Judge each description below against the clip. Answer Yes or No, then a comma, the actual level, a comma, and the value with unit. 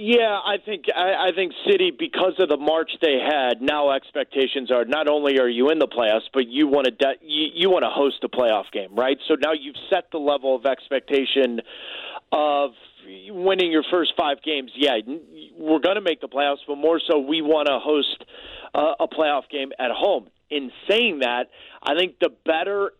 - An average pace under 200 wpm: No, fast, 205 wpm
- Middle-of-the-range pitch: Yes, medium, 150 Hz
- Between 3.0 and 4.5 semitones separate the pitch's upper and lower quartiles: No, average, 4.9 semitones